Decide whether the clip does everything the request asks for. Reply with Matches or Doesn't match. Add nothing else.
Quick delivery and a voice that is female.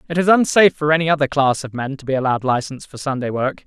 Doesn't match